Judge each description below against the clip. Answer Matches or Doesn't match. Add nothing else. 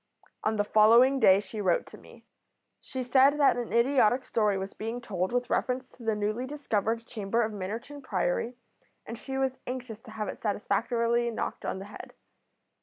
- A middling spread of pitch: Matches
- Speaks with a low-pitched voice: Doesn't match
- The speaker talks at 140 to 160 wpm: Doesn't match